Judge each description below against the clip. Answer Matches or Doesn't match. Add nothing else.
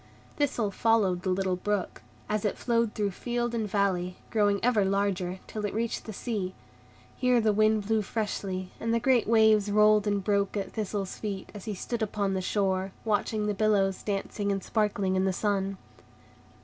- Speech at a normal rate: Matches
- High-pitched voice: Matches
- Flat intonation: Matches